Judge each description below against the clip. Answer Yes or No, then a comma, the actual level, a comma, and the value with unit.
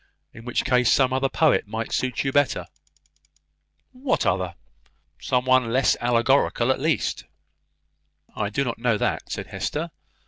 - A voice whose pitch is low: Yes, low, 125 Hz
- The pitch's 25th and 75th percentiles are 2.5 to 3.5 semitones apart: Yes, average, 2.8 semitones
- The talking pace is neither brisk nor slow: Yes, average, 150 wpm